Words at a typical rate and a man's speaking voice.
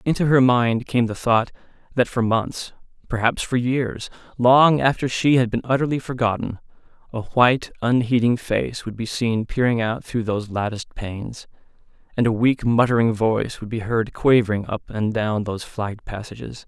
Yes: average, 170 wpm; male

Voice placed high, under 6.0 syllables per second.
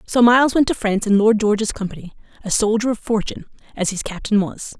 No: high, 215 Hz; 6.5 syllables/s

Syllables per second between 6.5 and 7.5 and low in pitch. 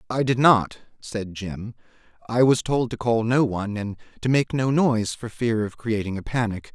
No: 4.9 syllables/s; low, 115 Hz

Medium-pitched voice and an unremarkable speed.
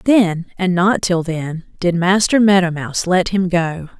Yes: medium, 180 Hz; average, 150 wpm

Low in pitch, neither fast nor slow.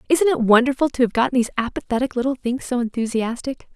No: very high, 250 Hz; average, 190 wpm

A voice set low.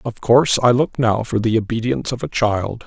Yes: low, 115 Hz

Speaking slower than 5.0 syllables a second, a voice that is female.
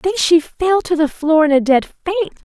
Yes: 4.4 syllables/s; female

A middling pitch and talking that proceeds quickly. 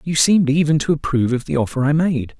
Yes: medium, 145 Hz; fast, 250 wpm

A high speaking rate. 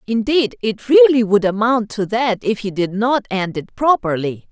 No: average, 185 wpm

